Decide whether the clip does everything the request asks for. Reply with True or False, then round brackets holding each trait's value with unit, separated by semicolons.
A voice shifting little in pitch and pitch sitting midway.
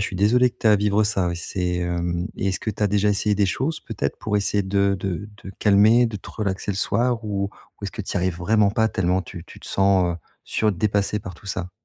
False (2.2 semitones; 100 Hz)